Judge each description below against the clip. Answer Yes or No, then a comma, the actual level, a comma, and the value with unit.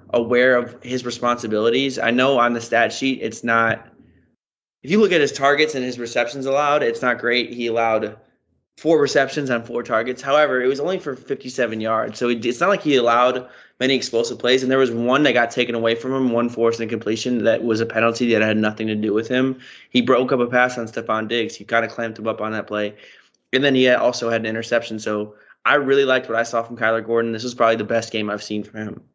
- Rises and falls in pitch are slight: Yes, narrow, 2.1 semitones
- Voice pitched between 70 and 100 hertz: No, low, 120 Hz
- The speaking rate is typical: No, fast, 240 wpm